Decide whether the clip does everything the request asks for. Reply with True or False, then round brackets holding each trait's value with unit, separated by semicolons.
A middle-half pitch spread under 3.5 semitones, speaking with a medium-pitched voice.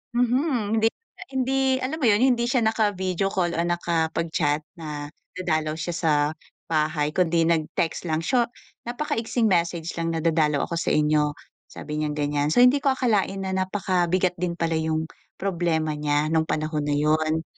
False (5.0 semitones; 170 Hz)